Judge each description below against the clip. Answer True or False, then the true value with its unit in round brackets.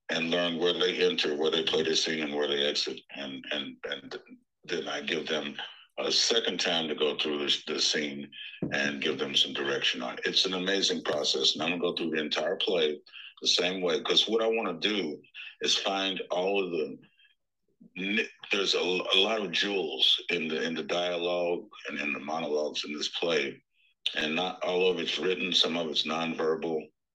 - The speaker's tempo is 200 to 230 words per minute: True (205 wpm)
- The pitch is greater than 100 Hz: False (95 Hz)